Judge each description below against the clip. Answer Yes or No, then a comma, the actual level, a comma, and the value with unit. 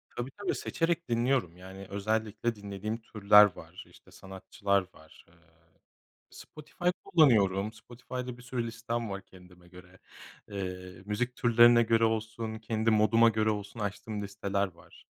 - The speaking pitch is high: No, low, 110 Hz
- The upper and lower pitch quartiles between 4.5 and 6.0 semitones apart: No, average, 3.1 semitones